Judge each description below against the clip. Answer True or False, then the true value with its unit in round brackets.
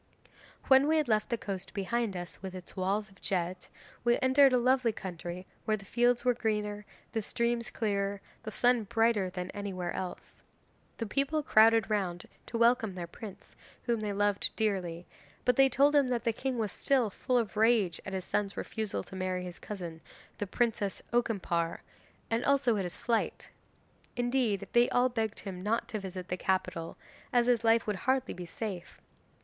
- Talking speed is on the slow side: False (185 wpm)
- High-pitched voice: True (215 Hz)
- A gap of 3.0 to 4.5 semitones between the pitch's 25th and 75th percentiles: True (4.1 semitones)